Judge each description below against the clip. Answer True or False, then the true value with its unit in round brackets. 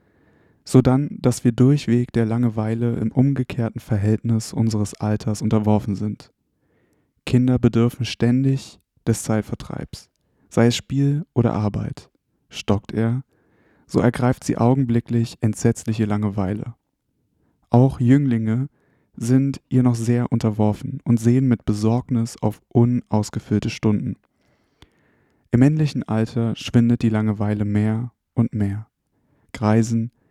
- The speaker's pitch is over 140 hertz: False (115 Hz)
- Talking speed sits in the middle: False (110 wpm)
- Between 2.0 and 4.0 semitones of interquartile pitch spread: True (2.5 semitones)